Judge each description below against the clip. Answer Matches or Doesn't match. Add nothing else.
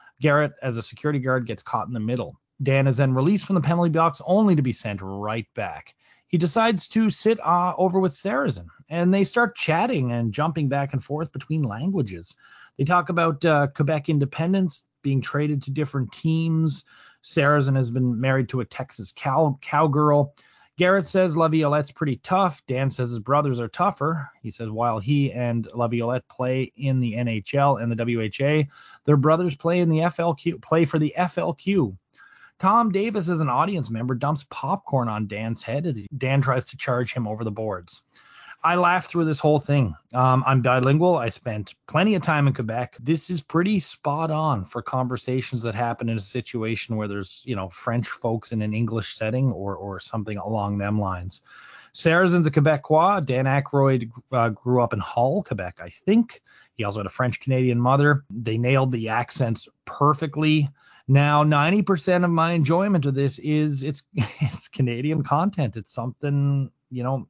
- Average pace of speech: Matches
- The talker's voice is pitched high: Doesn't match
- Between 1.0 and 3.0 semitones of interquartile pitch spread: Doesn't match